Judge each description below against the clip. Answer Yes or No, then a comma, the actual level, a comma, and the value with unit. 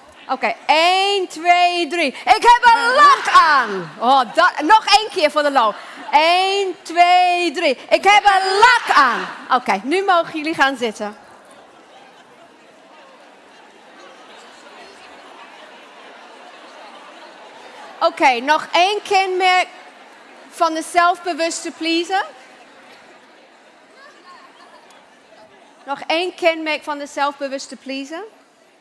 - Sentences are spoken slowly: Yes, slow, 105 wpm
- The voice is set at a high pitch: Yes, very high, 345 Hz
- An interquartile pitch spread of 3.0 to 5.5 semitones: Yes, average, 4.3 semitones